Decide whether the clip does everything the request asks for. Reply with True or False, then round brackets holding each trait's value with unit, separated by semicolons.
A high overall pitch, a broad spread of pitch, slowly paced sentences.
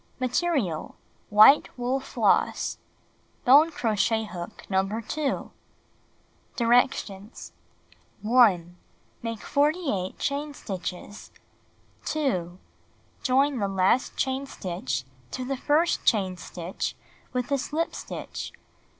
True (235 Hz; 6.2 semitones; 95 wpm)